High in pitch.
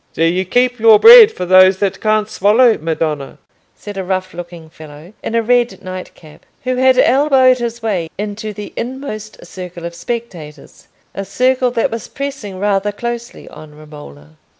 Yes: high, 205 Hz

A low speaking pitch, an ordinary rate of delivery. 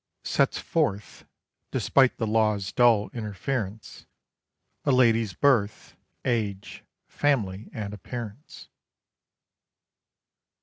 No: low, 110 Hz; slow, 80 wpm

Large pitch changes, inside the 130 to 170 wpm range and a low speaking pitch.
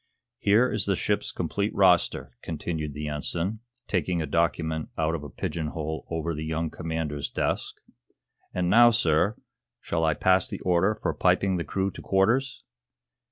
No: average, 3.5 semitones; average, 160 wpm; very low, 85 Hz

